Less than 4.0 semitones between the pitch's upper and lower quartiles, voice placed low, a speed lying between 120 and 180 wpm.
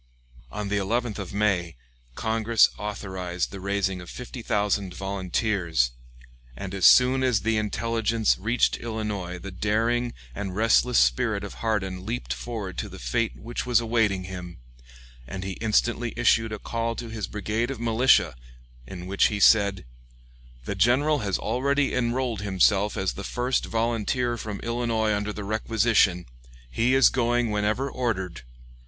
Yes: average, 3.3 semitones; low, 105 Hz; average, 150 wpm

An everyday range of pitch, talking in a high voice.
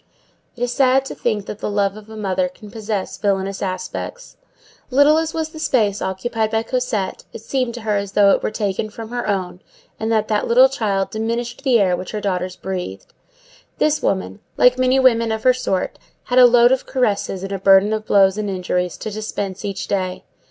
Yes: average, 3.9 semitones; high, 215 Hz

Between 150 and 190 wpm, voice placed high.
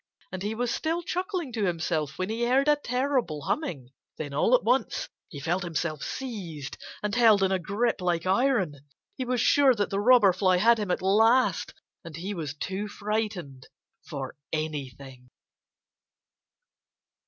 Yes: average, 160 wpm; high, 200 Hz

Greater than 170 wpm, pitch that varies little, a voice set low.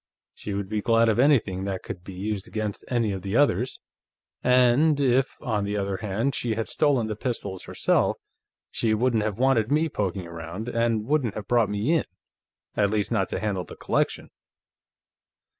No: average, 180 wpm; average, 3.7 semitones; low, 110 Hz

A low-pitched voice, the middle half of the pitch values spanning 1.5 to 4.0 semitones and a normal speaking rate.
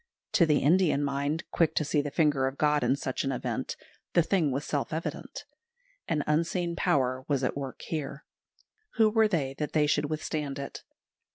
No: medium, 150 Hz; average, 2.7 semitones; average, 185 wpm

